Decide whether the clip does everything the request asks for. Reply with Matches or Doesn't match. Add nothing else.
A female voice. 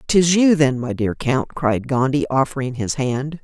Matches